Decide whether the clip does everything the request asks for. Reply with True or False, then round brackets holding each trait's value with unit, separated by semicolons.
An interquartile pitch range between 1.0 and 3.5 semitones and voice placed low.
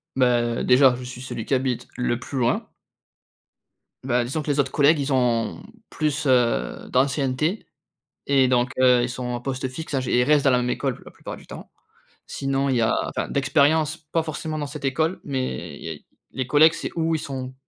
True (2.8 semitones; 130 Hz)